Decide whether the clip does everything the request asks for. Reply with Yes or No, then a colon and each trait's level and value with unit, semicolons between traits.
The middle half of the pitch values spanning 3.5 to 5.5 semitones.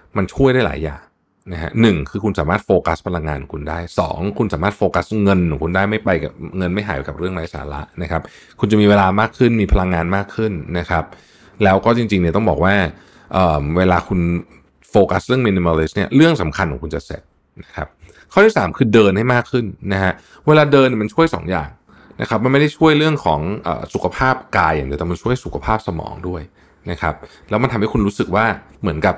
Yes: average, 4.8 semitones